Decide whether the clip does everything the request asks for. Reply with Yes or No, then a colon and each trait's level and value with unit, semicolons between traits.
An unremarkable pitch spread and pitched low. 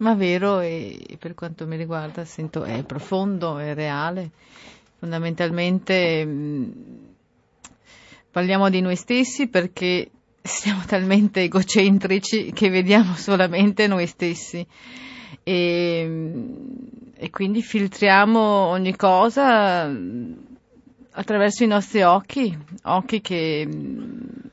No: average, 4.2 semitones; high, 190 Hz